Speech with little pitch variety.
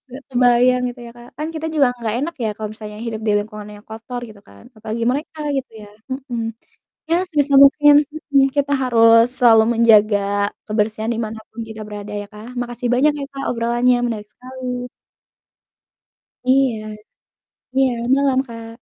No: average, 3.2 semitones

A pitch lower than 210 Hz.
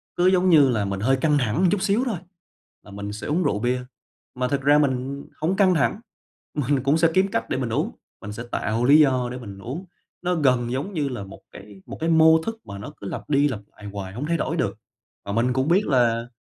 Yes: low, 135 Hz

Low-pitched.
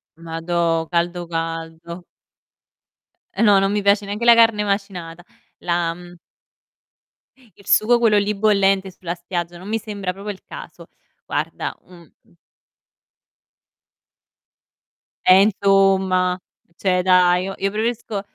No: high, 190 Hz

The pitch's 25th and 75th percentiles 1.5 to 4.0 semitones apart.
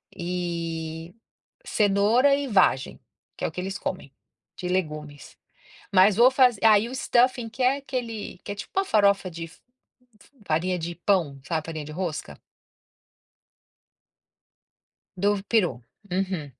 No: average, 5.0 semitones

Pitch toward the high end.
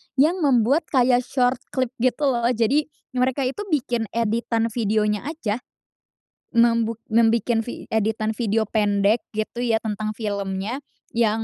Yes: high, 230 Hz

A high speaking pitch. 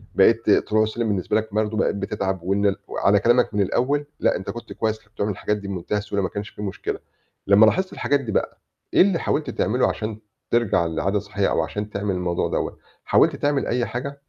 No: low, 105 Hz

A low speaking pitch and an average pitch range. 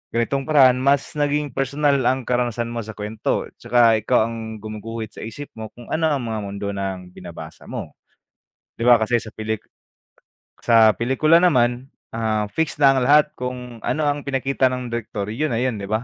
Yes: low, 120 Hz; average, 3.7 semitones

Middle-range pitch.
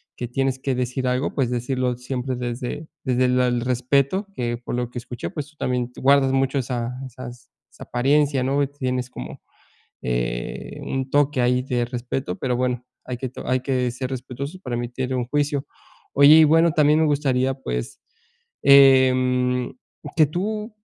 No: low, 130 Hz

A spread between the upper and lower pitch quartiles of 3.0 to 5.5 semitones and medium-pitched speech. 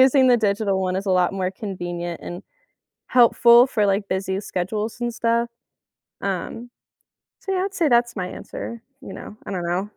No: average, 4.1 semitones; high, 205 Hz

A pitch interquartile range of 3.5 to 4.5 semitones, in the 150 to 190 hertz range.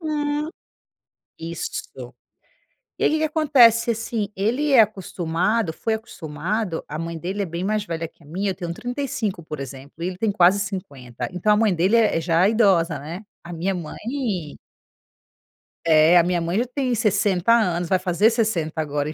No: average, 5.1 semitones; medium, 185 Hz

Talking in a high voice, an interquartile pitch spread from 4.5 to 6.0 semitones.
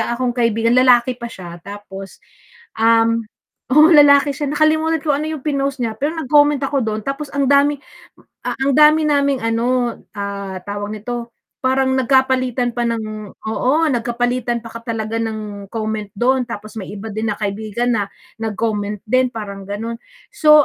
No: high, 235 Hz; average, 4.0 semitones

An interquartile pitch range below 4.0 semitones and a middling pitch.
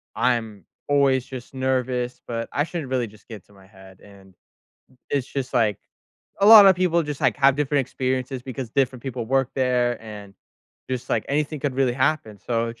No: average, 3.1 semitones; low, 130 Hz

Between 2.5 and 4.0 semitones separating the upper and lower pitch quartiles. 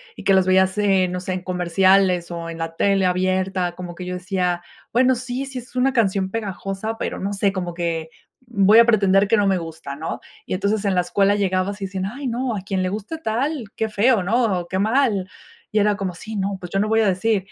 Yes: average, 3.0 semitones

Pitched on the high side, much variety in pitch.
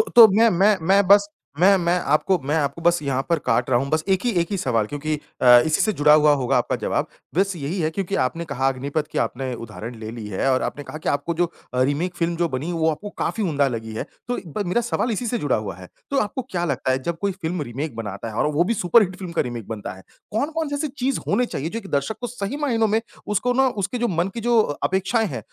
No: medium, 170 Hz; wide, 6.8 semitones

